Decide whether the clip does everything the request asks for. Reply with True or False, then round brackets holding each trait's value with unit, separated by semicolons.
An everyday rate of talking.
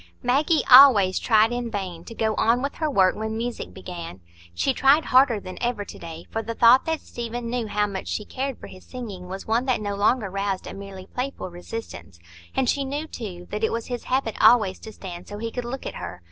False (230 wpm)